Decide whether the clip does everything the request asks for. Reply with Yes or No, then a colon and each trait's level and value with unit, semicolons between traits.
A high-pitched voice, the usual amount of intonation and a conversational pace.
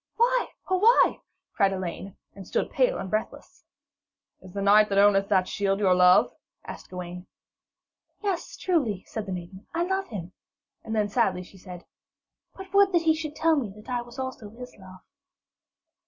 No: high, 210 Hz; wide, 9.0 semitones; average, 175 wpm